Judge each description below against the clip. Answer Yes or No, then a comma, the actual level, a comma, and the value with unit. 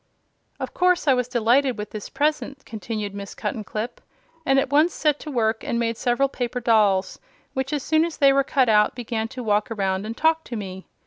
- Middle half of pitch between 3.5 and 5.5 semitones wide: Yes, average, 4.3 semitones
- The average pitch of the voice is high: Yes, high, 240 Hz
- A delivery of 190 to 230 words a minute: Yes, fast, 205 wpm